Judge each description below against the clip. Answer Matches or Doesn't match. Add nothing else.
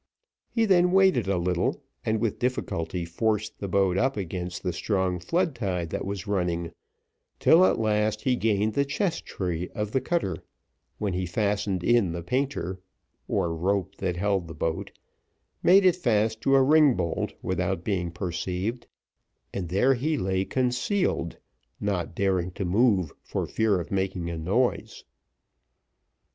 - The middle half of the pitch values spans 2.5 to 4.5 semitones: Doesn't match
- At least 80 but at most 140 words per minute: Doesn't match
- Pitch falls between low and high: Doesn't match